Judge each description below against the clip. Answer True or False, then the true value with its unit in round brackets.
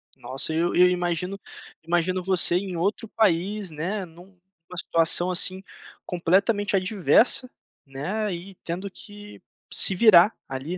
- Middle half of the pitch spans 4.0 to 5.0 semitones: False (2.7 semitones)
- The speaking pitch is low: False (185 Hz)